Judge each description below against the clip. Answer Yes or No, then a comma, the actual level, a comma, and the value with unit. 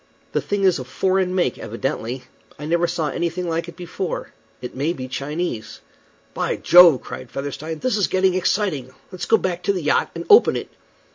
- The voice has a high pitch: No, medium, 170 Hz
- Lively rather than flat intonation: No, average, 4.8 semitones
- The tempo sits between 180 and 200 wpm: Yes, average, 190 wpm